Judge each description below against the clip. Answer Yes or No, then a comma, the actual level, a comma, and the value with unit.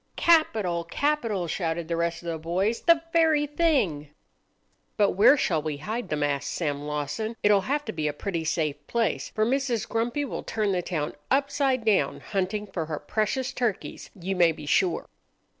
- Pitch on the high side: Yes, high, 195 Hz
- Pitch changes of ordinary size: No, wide, 6.9 semitones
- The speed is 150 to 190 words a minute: Yes, average, 175 wpm